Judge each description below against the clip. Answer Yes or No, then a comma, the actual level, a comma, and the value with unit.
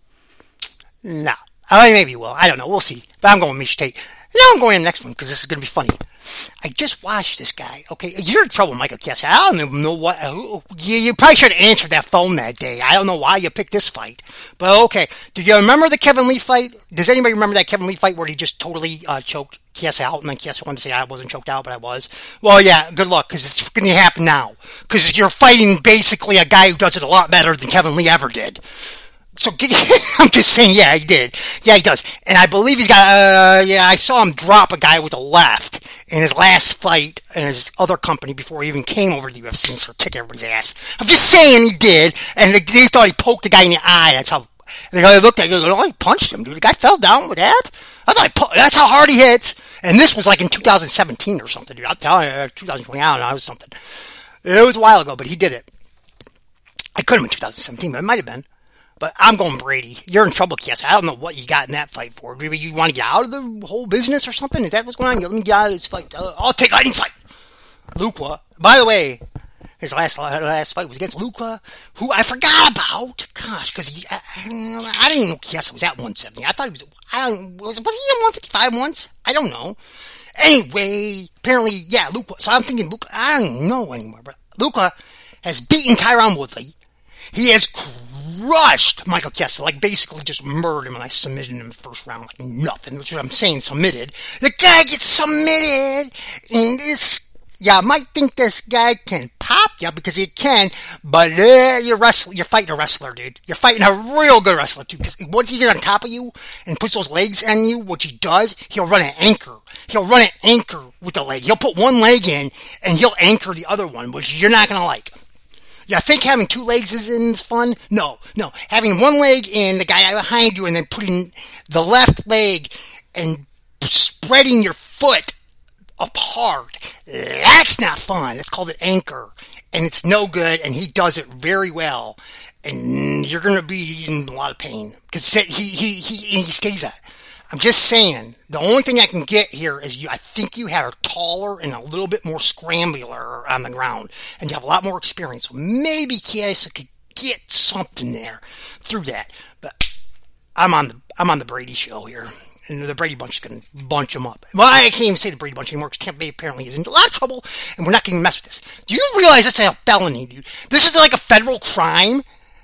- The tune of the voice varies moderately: No, wide, 6.7 semitones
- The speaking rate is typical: No, fast, 235 wpm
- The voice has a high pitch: Yes, high, 195 Hz